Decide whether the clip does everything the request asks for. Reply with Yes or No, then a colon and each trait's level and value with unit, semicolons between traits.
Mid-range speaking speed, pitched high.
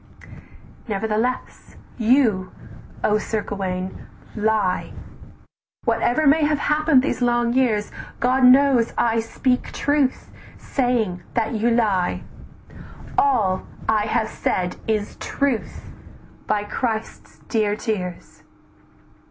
No: slow, 100 wpm; high, 225 Hz